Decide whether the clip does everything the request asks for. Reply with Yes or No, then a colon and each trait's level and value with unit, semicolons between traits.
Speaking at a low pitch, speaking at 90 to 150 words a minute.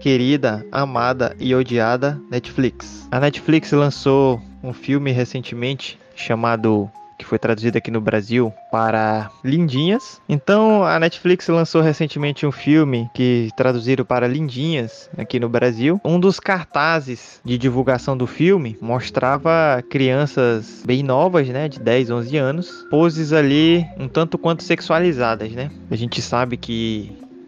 Yes: low, 130 Hz; average, 135 wpm